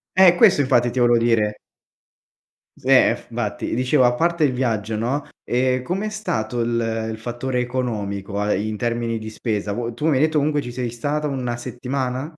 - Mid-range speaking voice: No, low, 120 Hz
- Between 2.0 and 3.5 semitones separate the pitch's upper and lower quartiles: Yes, average, 2.9 semitones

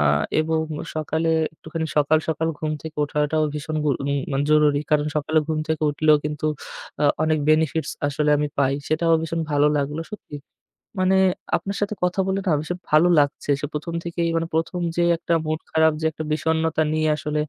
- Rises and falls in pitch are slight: Yes, narrow, 1.4 semitones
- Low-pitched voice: No, medium, 155 Hz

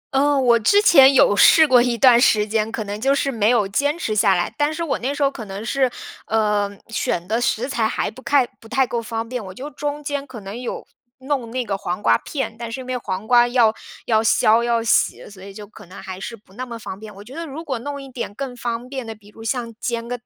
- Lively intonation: No, average, 3.7 semitones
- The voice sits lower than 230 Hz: No, high, 235 Hz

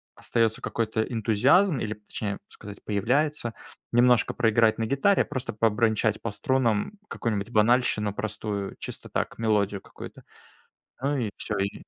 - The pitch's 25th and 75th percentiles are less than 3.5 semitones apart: Yes, average, 2.8 semitones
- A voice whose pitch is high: No, low, 110 Hz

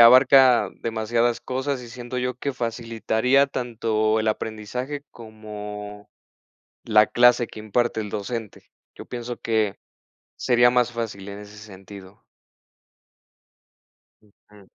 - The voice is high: No, low, 115 Hz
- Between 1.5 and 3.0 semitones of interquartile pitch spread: Yes, narrow, 2.5 semitones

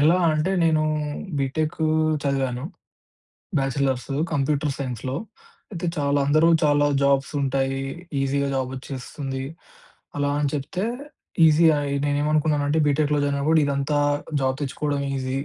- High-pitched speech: No, medium, 140 Hz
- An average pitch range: No, narrow, 2.0 semitones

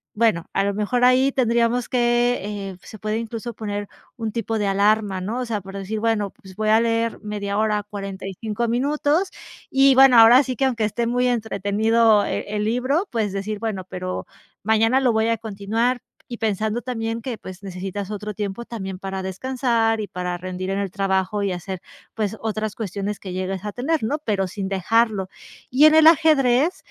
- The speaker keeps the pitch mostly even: No, average, 3.2 semitones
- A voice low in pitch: No, high, 220 Hz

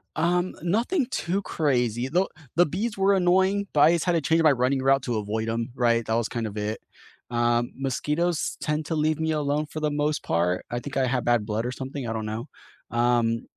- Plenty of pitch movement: Yes, wide, 5.7 semitones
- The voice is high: No, low, 135 Hz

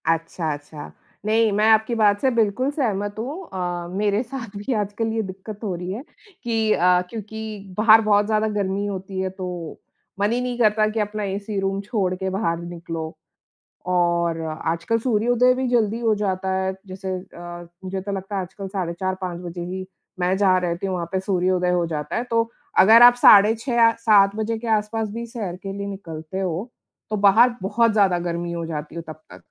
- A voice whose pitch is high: Yes, high, 200 Hz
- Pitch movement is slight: No, average, 3.5 semitones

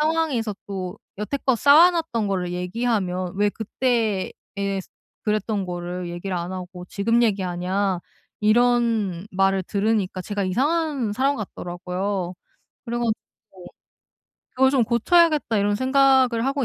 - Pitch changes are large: No, average, 4.8 semitones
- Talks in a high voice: Yes, high, 210 Hz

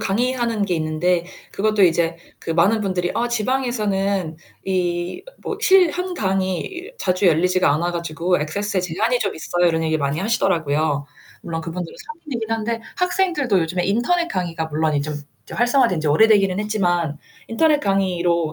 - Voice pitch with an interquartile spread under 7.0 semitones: Yes, average, 5.3 semitones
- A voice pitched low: No, medium, 185 Hz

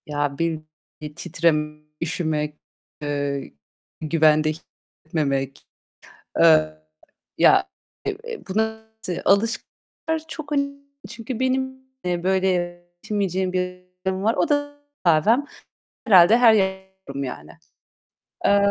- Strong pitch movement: Yes, wide, 6.0 semitones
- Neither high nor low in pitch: Yes, medium, 180 Hz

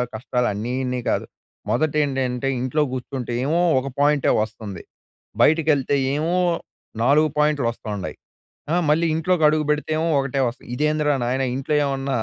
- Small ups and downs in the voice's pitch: No, average, 3.5 semitones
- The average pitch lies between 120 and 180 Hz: Yes, medium, 140 Hz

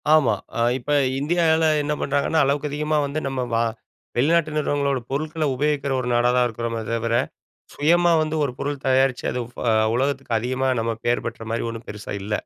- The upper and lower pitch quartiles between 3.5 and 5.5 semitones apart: Yes, average, 3.9 semitones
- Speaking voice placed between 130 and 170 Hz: Yes, low, 135 Hz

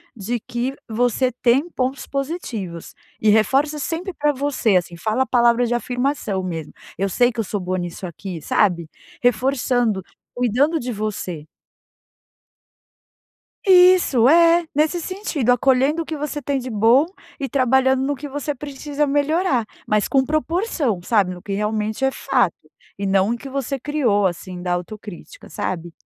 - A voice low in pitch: No, high, 245 Hz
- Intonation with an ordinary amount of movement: No, wide, 5.7 semitones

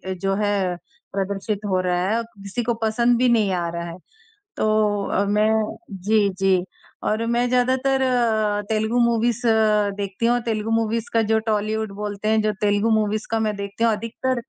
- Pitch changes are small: Yes, narrow, 2.3 semitones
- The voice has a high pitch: Yes, high, 215 Hz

